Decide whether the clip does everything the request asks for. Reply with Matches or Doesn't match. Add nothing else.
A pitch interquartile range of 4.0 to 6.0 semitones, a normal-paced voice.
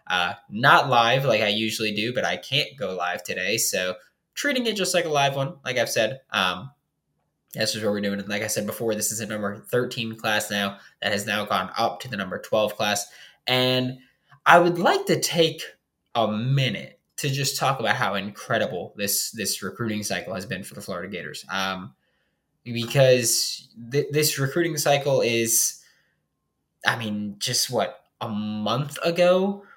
Matches